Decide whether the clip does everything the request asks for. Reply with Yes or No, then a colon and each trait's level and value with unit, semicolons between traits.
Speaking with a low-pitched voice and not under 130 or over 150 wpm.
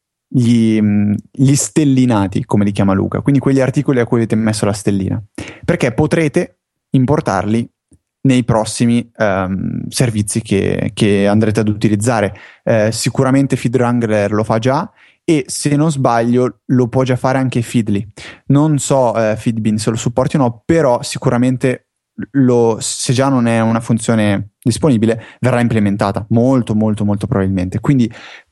Yes: low, 120 Hz; average, 145 wpm